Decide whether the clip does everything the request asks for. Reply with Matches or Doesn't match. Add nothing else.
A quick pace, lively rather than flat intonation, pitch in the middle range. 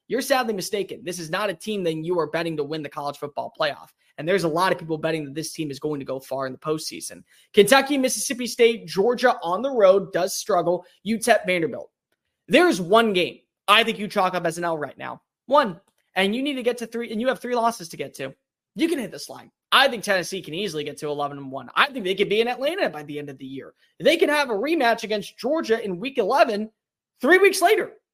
Doesn't match